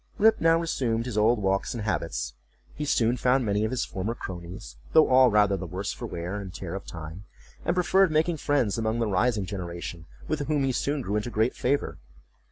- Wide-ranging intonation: Yes, wide, 5.9 semitones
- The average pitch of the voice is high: No, low, 110 Hz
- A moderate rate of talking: No, fast, 210 wpm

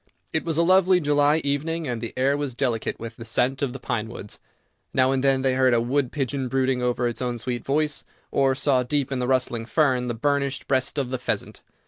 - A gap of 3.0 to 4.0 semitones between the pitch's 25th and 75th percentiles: No, narrow, 2.6 semitones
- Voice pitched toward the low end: Yes, low, 130 Hz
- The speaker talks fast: Yes, fast, 220 wpm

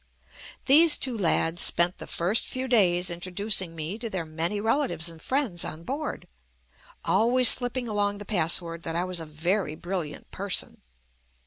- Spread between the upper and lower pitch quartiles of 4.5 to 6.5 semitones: Yes, average, 5.2 semitones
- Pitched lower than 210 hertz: Yes, medium, 185 Hz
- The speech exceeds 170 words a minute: No, average, 160 wpm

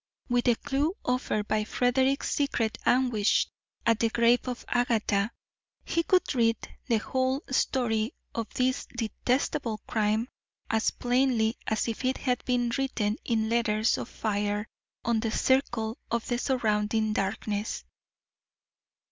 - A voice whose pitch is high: Yes, high, 235 Hz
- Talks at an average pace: No, slow, 130 wpm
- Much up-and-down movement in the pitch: No, narrow, 2.5 semitones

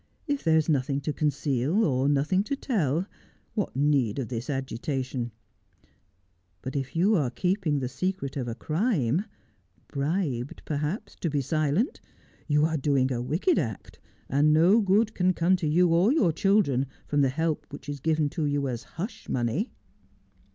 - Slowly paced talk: No, average, 170 wpm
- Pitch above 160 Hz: No, medium, 150 Hz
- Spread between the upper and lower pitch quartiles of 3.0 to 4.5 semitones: No, average, 5.1 semitones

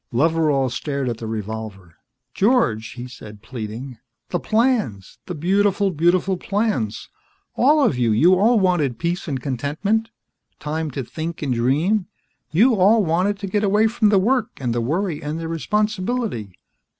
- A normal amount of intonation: No, wide, 8.5 semitones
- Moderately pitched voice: Yes, medium, 165 Hz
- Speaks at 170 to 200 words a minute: No, average, 155 wpm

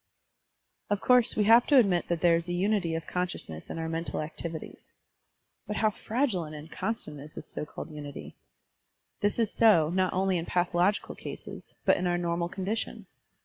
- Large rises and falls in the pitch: No, average, 4.1 semitones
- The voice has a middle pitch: Yes, medium, 175 Hz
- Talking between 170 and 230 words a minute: Yes, average, 180 wpm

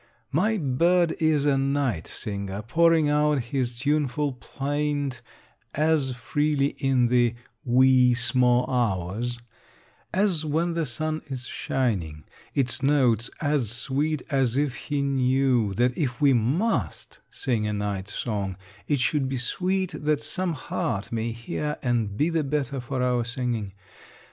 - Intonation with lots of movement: No, average, 3.7 semitones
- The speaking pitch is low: Yes, low, 130 Hz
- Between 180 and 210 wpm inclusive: No, average, 140 wpm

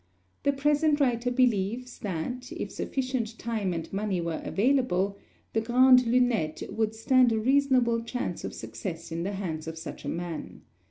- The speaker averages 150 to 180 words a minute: Yes, average, 160 wpm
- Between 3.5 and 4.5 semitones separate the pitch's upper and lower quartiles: No, average, 5.0 semitones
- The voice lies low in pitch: No, high, 230 Hz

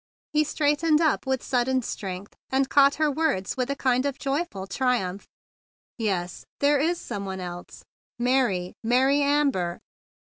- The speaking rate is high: No, average, 155 wpm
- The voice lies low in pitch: No, very high, 260 Hz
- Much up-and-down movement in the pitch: Yes, wide, 6.6 semitones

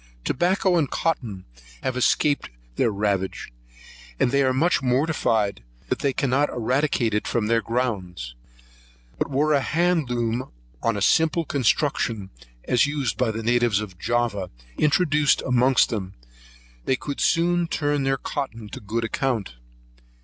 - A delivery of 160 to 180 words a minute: No, average, 140 wpm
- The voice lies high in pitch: No, low, 125 Hz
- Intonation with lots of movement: No, average, 4.7 semitones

